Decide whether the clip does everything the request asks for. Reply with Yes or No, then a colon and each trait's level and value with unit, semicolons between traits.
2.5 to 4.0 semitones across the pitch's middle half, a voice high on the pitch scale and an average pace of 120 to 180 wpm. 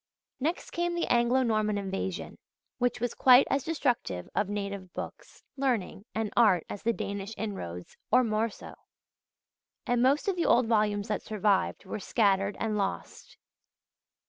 Yes: average, 3.7 semitones; high, 215 Hz; average, 150 wpm